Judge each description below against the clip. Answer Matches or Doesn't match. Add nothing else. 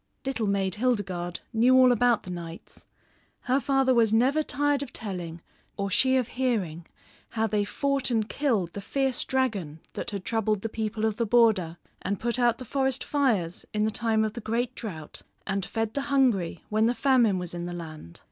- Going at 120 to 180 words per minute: Doesn't match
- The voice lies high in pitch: Matches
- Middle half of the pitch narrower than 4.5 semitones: Doesn't match